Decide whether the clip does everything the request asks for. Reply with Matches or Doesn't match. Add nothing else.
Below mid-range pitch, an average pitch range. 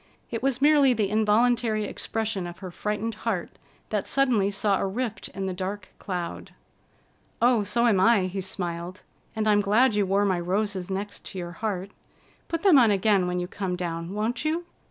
Doesn't match